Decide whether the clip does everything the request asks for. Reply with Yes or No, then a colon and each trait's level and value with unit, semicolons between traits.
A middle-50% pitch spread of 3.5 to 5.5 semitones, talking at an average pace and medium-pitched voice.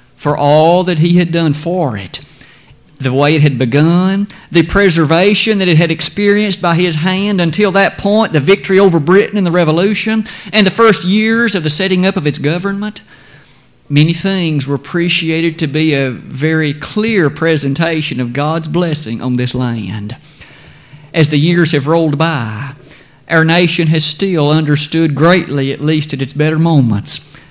Yes: average, 4.1 semitones; average, 170 wpm; medium, 160 Hz